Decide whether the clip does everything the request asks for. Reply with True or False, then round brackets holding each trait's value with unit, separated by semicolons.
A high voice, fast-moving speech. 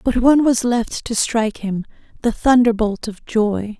False (230 Hz; 160 wpm)